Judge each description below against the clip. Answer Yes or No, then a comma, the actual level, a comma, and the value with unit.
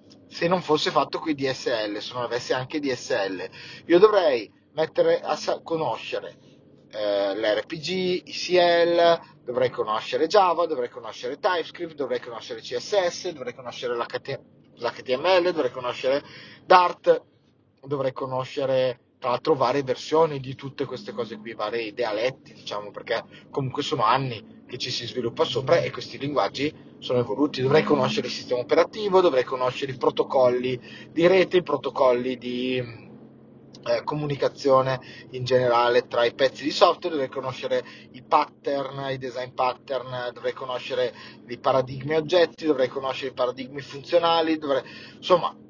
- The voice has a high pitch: No, medium, 140 Hz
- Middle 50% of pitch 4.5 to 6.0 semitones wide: Yes, wide, 5.6 semitones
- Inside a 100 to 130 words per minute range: No, average, 140 wpm